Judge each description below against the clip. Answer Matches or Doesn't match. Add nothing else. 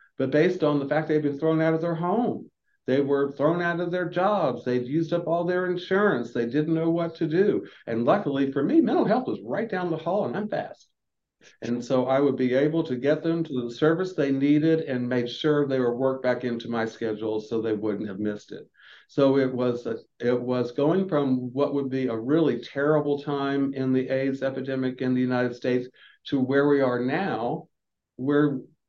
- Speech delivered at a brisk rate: Matches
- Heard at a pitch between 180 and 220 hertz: Doesn't match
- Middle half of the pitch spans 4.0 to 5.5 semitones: Matches